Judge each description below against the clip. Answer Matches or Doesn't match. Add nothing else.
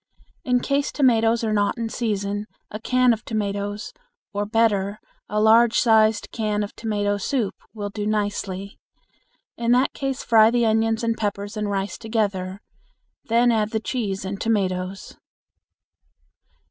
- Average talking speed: Matches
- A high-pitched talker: Matches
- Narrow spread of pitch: Matches